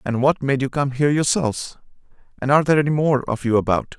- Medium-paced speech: No, fast, 210 wpm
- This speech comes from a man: Yes, male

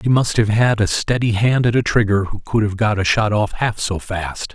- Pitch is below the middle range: Yes, low, 110 Hz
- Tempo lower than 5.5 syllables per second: Yes, 4.9 syllables/s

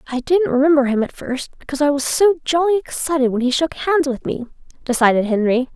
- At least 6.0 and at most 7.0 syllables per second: Yes, 6.1 syllables/s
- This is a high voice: Yes, very high, 280 Hz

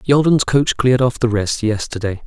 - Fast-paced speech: No, average, 185 wpm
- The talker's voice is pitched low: Yes, low, 120 Hz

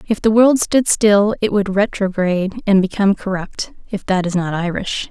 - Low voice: No, high, 200 Hz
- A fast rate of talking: No, average, 190 wpm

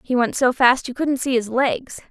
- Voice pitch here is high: Yes, very high, 250 Hz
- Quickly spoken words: Yes, fast, 255 wpm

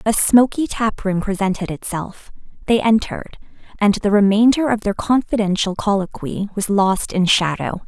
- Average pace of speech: Yes, average, 145 wpm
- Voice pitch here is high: Yes, high, 205 Hz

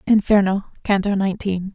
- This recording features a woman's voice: Yes, female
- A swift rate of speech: No, slow, 105 wpm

